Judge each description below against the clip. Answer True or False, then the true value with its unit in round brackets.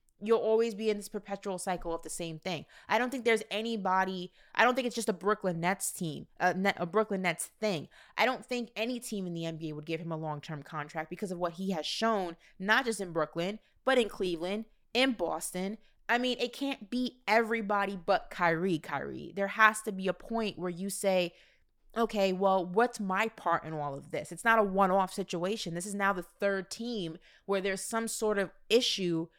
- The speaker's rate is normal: False (215 wpm)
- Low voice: False (195 Hz)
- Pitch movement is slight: False (3.9 semitones)